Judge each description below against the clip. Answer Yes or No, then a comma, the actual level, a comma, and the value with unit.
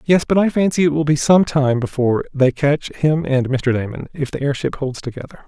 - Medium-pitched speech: Yes, medium, 145 Hz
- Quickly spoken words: Yes, fast, 230 wpm